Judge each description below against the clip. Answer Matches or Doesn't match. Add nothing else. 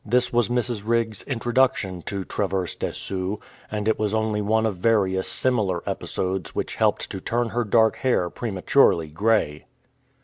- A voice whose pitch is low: Matches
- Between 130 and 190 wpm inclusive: Matches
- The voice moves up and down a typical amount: Matches